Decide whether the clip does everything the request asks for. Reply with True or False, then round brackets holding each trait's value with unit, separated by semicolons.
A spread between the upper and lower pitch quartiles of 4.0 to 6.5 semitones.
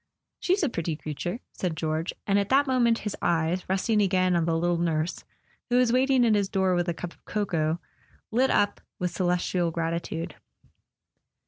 True (4.4 semitones)